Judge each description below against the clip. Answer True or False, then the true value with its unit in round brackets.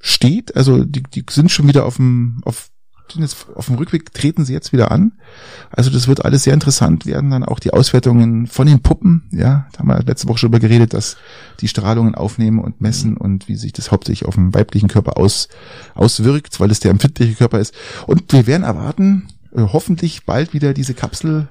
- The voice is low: True (125 Hz)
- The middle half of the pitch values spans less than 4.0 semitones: False (4.5 semitones)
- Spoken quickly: True (210 wpm)